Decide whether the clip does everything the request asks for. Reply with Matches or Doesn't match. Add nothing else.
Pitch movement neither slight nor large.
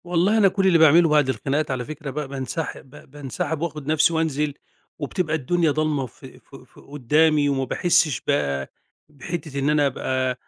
Matches